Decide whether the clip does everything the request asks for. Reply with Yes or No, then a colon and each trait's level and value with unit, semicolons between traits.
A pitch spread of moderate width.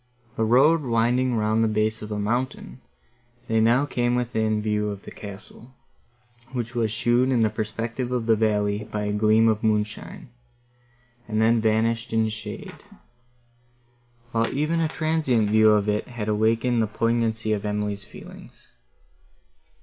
No: narrow, 2.1 semitones